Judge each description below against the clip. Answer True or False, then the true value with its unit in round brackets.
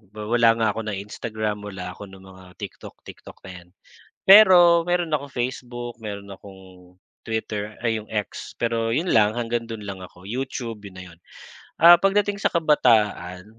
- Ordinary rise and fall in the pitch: True (4.0 semitones)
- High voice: False (110 Hz)